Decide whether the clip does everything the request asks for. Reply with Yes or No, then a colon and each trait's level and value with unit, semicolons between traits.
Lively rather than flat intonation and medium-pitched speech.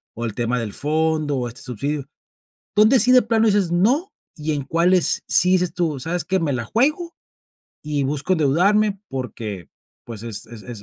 Yes: wide, 7.5 semitones; medium, 155 Hz